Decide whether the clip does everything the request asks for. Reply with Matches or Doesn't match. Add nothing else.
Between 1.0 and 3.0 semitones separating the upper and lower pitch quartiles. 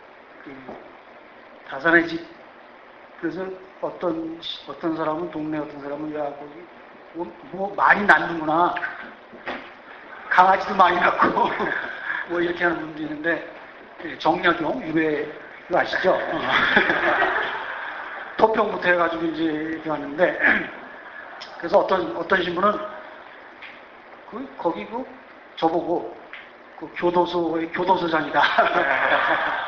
Matches